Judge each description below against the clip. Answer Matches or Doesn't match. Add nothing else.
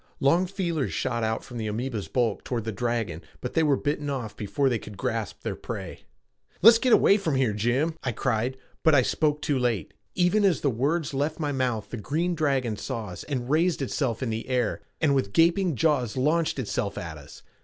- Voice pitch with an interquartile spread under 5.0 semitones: Doesn't match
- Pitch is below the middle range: Matches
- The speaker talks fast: Matches